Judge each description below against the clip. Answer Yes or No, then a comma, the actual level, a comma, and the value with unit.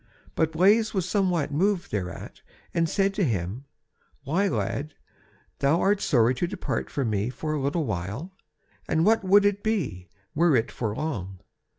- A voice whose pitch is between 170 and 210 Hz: No, medium, 160 Hz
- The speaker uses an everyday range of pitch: No, wide, 8.1 semitones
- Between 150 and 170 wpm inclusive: Yes, average, 165 wpm